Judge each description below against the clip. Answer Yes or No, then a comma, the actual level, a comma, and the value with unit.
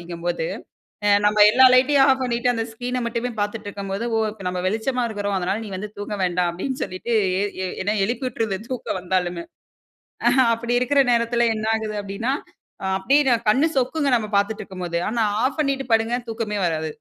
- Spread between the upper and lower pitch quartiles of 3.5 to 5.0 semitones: Yes, average, 4.2 semitones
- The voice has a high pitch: Yes, high, 220 Hz